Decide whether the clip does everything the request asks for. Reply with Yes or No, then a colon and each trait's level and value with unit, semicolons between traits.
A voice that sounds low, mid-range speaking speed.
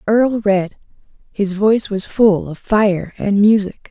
No: high, 205 Hz; average, 155 wpm